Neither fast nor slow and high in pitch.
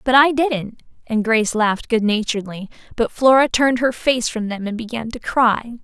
Yes: average, 195 wpm; high, 235 Hz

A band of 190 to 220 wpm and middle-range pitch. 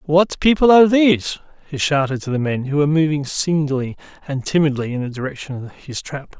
Yes: average, 195 wpm; medium, 150 Hz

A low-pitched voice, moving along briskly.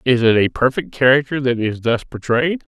No: low, 130 Hz; average, 195 wpm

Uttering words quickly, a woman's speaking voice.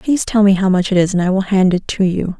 Yes: fast, 350 wpm; female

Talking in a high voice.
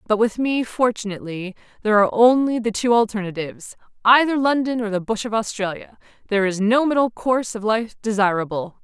Yes: high, 220 Hz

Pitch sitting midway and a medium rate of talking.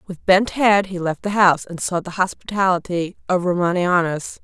Yes: medium, 180 Hz; average, 175 wpm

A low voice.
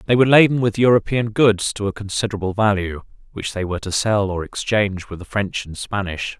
Yes: low, 105 Hz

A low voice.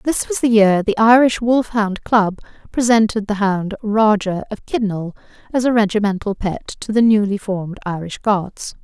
No: high, 210 Hz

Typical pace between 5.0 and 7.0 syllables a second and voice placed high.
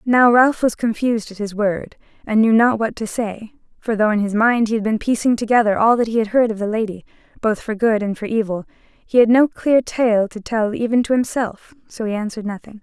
Yes: 5.5 syllables/s; high, 225 Hz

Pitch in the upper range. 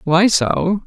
No: medium, 180 Hz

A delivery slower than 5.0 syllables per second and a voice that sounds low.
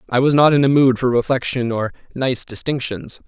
No: 5.4 syllables/s; low, 125 Hz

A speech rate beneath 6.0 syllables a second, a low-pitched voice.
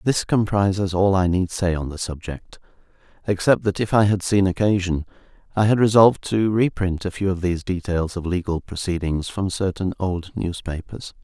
Yes: 5.1 syllables/s; very low, 95 Hz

